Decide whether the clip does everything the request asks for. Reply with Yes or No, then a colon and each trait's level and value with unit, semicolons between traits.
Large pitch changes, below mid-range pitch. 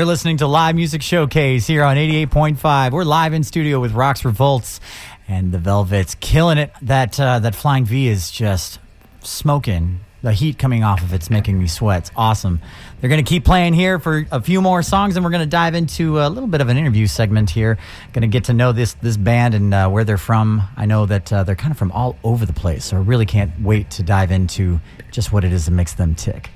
Yes: wide, 6.8 semitones; low, 115 Hz